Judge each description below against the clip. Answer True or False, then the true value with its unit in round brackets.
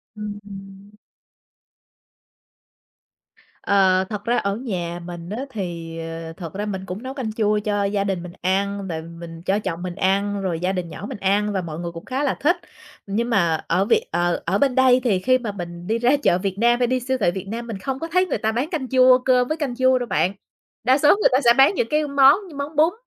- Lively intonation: True (5.7 semitones)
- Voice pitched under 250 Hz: True (205 Hz)